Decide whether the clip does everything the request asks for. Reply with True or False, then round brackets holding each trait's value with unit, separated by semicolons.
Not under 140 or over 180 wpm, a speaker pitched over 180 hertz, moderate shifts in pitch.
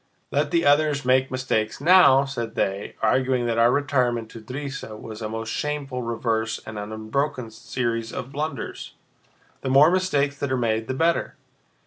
False (165 wpm; 125 Hz; 3.9 semitones)